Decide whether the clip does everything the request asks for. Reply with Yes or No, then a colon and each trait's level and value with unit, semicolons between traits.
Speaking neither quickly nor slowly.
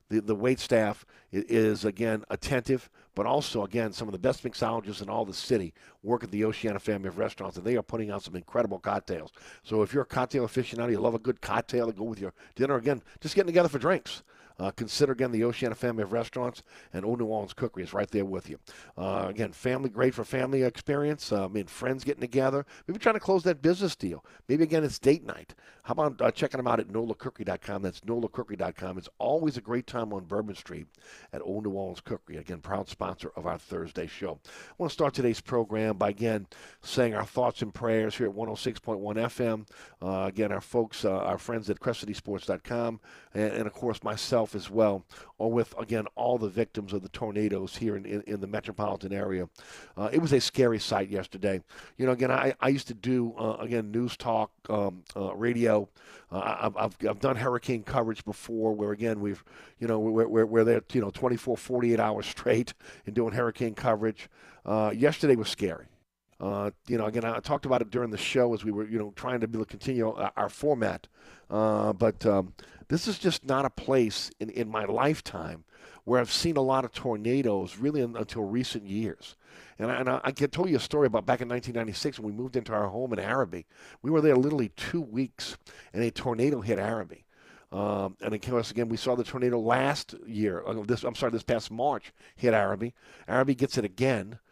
No: fast, 215 wpm